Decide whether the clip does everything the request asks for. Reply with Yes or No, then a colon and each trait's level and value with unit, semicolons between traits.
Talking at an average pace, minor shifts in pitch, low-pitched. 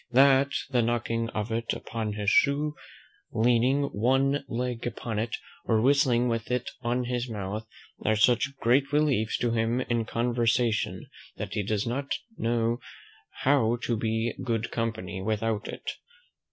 Yes: average, 145 wpm; narrow, 2.0 semitones; low, 115 Hz